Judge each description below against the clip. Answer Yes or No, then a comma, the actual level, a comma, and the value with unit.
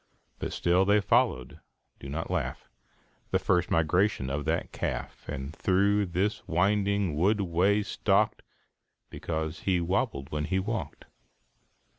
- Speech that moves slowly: Yes, slow, 130 wpm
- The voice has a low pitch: Yes, very low, 90 Hz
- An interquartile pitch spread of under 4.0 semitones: No, average, 4.5 semitones